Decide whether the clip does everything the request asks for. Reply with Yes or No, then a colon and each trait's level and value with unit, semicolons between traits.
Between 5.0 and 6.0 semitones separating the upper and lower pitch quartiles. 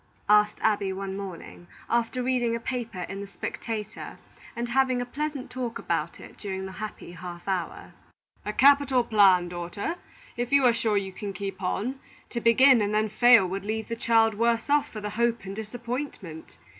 No: average, 3.7 semitones